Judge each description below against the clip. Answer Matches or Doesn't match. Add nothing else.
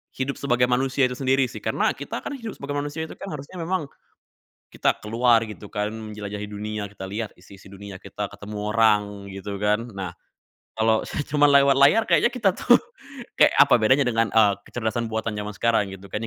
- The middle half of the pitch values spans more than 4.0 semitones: Matches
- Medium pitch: Doesn't match